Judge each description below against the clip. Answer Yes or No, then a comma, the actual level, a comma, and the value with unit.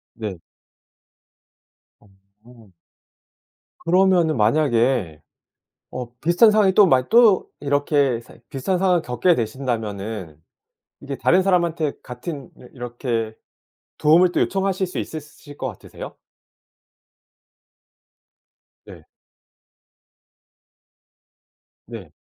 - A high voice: No, medium, 140 Hz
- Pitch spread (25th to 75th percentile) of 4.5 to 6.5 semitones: No, wide, 7.2 semitones